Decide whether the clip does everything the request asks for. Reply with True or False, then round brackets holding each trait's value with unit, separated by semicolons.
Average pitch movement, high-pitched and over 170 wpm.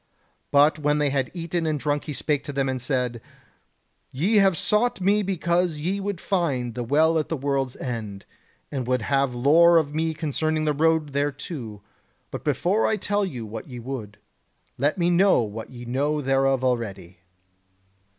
False (4.6 semitones; 145 Hz; 180 wpm)